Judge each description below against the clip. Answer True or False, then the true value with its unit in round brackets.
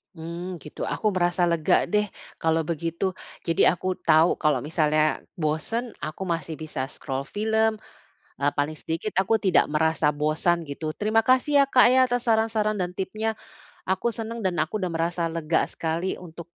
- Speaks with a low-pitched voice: False (170 Hz)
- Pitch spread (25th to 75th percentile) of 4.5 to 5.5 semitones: True (5.1 semitones)